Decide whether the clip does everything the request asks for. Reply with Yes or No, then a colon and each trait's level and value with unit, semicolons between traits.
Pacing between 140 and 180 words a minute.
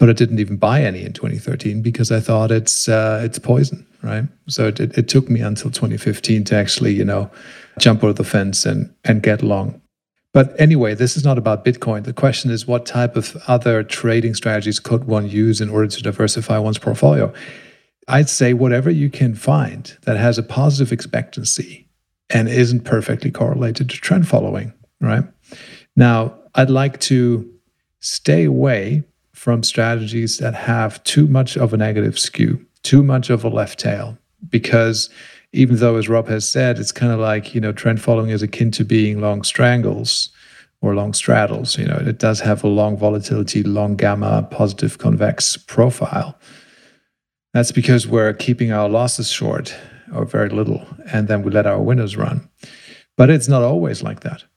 Yes: average, 175 wpm